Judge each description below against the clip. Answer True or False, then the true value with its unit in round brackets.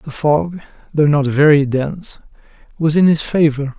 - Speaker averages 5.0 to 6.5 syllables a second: False (4.7 syllables/s)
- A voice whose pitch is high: False (150 Hz)